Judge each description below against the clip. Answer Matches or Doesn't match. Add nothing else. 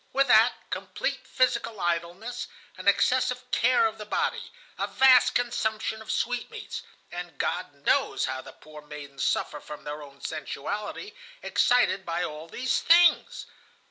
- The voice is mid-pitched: Doesn't match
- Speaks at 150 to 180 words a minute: Doesn't match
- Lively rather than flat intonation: Matches